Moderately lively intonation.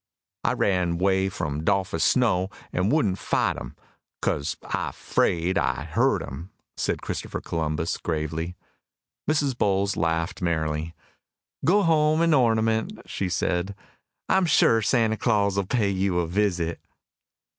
Yes: average, 4.8 semitones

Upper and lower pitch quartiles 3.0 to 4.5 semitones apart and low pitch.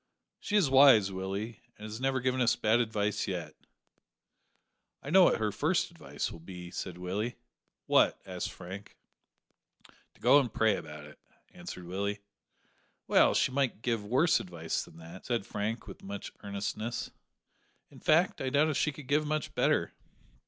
No: wide, 5.4 semitones; low, 110 Hz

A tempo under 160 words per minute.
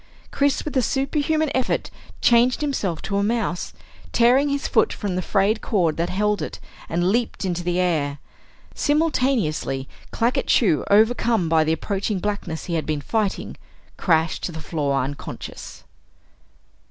Yes: average, 150 wpm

